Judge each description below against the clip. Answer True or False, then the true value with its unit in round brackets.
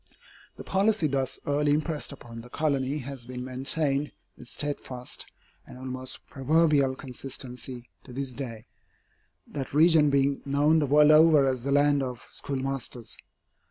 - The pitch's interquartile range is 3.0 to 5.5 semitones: False (2.4 semitones)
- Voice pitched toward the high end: False (140 Hz)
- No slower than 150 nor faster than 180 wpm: False (140 wpm)